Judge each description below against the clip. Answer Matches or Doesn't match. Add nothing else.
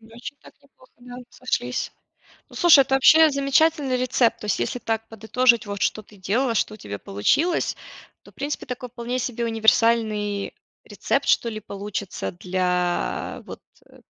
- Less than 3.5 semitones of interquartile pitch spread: Doesn't match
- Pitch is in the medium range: Doesn't match